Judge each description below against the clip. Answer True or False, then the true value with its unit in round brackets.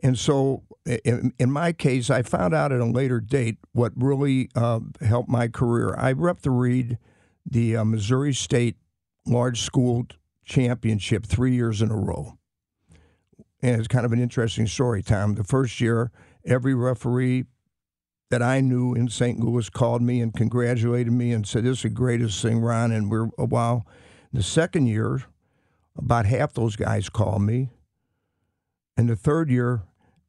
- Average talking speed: True (165 wpm)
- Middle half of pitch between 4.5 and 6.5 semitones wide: False (2.4 semitones)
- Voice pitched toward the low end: True (120 Hz)